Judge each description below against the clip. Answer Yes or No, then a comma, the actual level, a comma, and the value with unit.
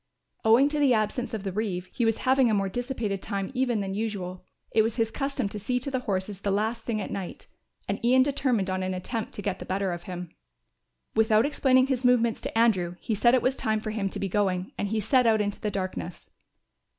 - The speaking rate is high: Yes, fast, 235 wpm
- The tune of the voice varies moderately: Yes, average, 3.9 semitones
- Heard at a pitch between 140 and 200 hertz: No, high, 215 Hz